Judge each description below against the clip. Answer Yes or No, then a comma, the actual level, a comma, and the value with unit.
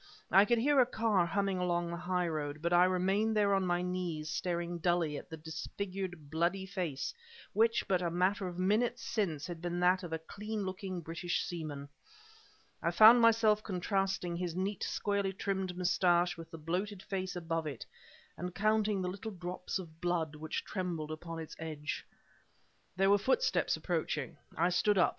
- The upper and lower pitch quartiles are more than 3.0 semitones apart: No, average, 2.7 semitones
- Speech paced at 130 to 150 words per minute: No, average, 175 wpm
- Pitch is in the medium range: Yes, medium, 180 Hz